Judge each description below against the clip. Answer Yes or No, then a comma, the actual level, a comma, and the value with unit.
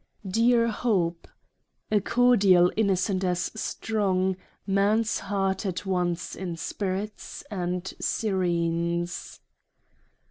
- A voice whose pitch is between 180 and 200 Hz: Yes, high, 190 Hz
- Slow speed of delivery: Yes, slow, 85 wpm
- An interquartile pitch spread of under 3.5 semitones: Yes, average, 2.9 semitones